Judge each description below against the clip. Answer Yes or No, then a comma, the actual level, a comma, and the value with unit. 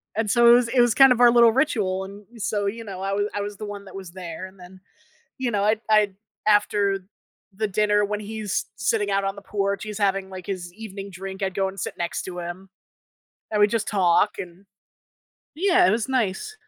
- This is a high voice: Yes, high, 205 Hz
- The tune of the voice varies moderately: No, narrow, 2.2 semitones